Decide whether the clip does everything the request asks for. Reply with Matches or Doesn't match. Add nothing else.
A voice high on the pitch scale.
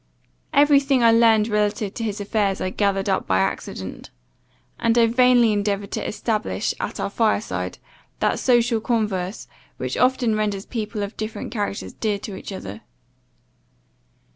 Matches